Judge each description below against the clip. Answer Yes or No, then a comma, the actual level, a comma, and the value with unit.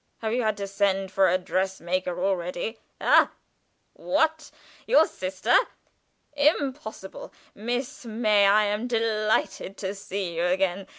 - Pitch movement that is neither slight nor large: Yes, average, 3.2 semitones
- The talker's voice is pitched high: Yes, high, 200 Hz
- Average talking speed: No, slow, 130 wpm